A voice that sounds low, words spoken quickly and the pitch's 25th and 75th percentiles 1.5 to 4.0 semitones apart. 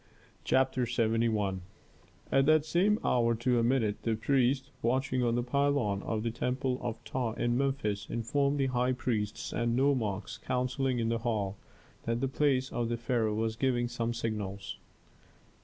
No: low, 120 Hz; average, 160 wpm; average, 2.7 semitones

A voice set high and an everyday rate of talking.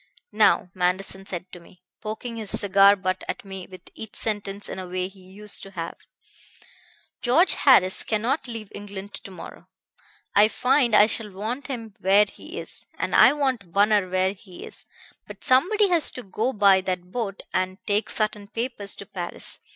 Yes: high, 205 Hz; average, 180 wpm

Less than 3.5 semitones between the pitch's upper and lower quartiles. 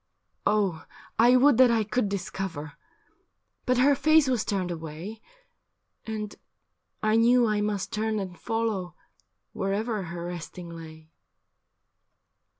No: average, 4.5 semitones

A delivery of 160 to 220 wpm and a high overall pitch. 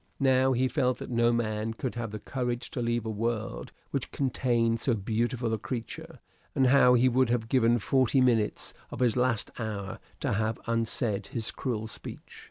No: average, 180 wpm; low, 120 Hz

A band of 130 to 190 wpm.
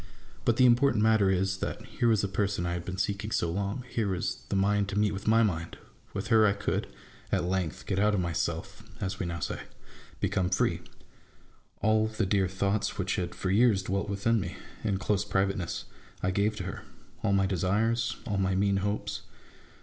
No: fast, 205 wpm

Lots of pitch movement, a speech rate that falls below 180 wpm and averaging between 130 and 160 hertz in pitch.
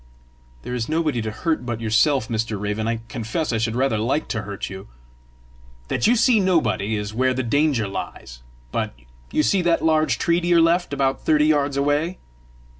No: wide, 6.1 semitones; average, 190 wpm; low, 135 Hz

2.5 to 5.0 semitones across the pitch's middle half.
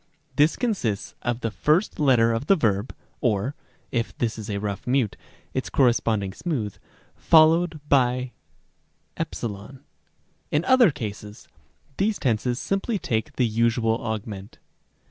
No: wide, 5.6 semitones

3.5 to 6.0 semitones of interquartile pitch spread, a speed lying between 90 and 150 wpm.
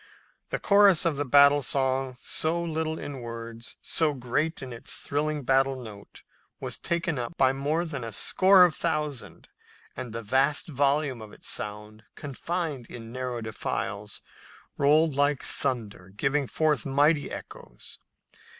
Yes: average, 4.1 semitones; average, 140 wpm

